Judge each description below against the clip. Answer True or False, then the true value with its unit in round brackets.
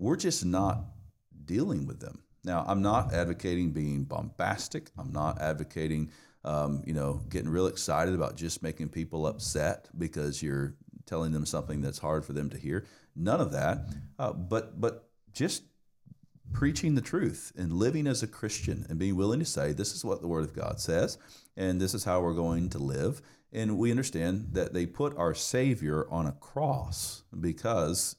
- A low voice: True (90 Hz)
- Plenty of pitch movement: True (6.2 semitones)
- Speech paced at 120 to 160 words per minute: False (180 wpm)